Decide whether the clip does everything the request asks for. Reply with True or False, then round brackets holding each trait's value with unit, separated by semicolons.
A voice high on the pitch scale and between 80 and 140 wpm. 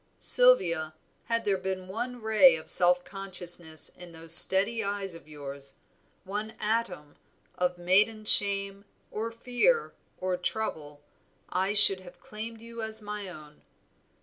True (195 Hz; 135 wpm)